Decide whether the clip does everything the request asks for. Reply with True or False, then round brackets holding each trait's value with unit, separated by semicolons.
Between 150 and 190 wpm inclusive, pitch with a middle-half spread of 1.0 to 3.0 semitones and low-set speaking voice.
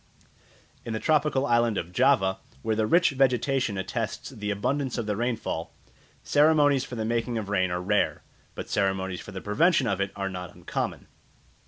False (175 wpm; 5.1 semitones; 110 Hz)